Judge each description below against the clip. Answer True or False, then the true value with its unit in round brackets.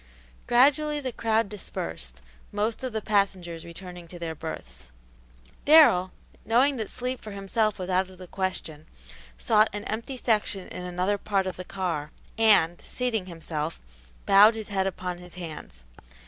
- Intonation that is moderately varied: True (4.1 semitones)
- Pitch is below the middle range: False (190 Hz)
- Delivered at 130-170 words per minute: True (155 wpm)